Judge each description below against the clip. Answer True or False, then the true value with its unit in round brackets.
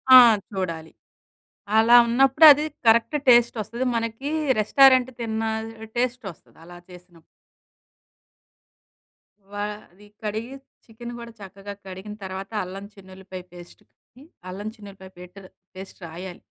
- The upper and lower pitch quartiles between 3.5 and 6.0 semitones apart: True (4.0 semitones)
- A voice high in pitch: True (205 Hz)